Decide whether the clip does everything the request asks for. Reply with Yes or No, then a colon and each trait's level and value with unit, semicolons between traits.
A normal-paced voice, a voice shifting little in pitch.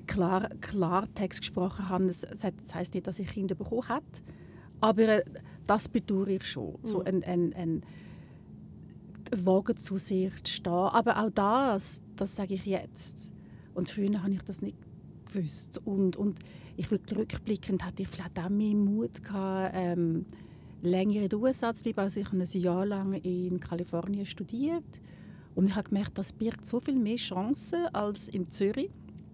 Yes: average, 160 wpm; narrow, 2.3 semitones